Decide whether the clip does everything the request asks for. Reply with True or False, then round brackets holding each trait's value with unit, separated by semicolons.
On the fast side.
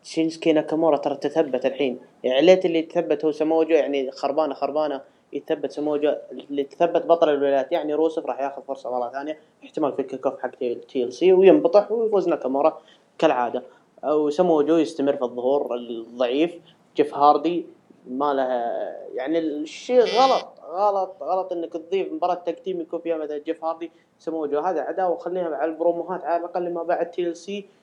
True (160 wpm)